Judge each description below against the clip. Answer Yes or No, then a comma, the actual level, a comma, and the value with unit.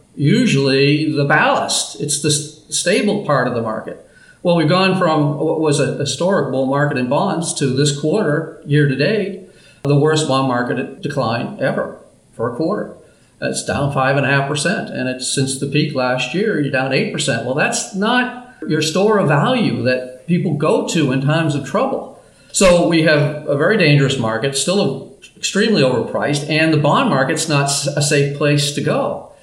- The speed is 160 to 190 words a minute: Yes, average, 185 wpm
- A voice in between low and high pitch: Yes, medium, 150 Hz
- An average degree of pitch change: Yes, average, 3.6 semitones